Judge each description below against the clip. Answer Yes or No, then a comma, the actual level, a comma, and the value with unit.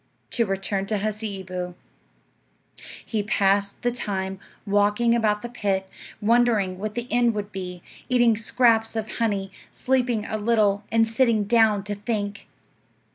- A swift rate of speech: No, slow, 135 wpm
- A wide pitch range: No, average, 2.7 semitones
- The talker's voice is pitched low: No, high, 210 Hz